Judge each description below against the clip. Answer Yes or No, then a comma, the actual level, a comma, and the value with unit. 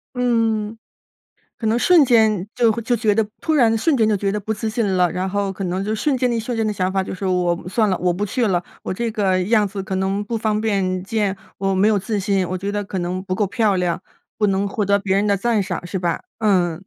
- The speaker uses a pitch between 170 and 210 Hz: Yes, high, 205 Hz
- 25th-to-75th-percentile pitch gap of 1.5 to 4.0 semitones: Yes, average, 2.8 semitones